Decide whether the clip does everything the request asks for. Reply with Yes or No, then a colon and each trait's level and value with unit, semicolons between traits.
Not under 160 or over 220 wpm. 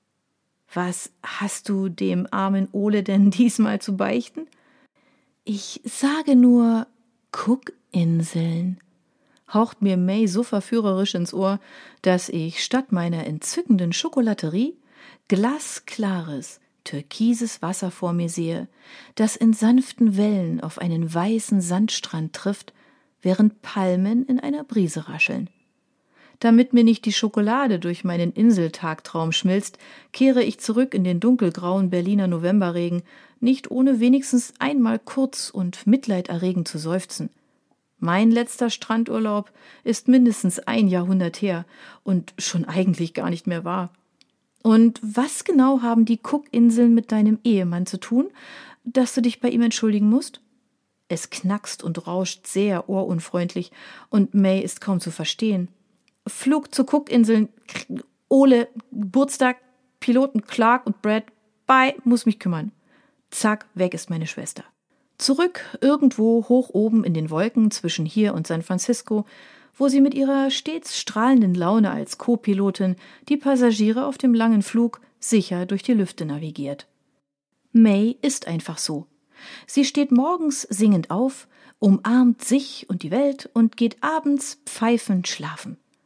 No: average, 130 wpm